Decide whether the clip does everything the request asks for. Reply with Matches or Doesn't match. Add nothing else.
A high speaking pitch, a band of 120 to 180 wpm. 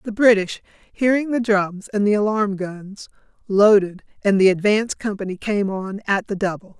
Matches